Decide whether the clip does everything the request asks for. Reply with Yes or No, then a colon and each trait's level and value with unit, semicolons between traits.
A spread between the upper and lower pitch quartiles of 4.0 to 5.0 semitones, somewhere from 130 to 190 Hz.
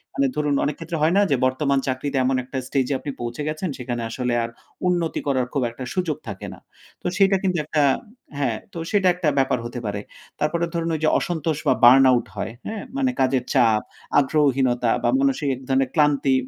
Yes: average, 4.4 semitones; medium, 140 Hz